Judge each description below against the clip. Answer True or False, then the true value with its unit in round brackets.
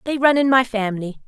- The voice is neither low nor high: False (240 Hz)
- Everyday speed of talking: False (235 wpm)